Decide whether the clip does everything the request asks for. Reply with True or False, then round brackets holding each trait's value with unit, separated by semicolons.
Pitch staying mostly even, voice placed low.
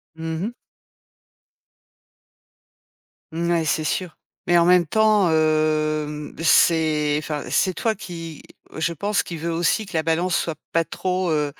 False (2.3 semitones; 165 Hz)